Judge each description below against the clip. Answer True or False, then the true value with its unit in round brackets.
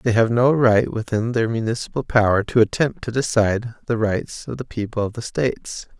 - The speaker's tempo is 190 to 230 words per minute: True (200 wpm)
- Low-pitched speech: True (115 Hz)